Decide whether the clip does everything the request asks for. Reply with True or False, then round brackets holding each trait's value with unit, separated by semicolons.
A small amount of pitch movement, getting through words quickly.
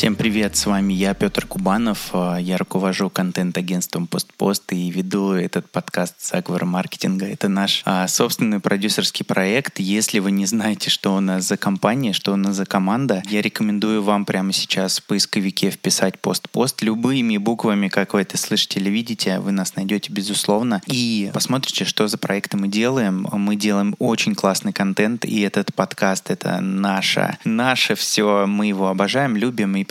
True (1.5 semitones; 165 wpm)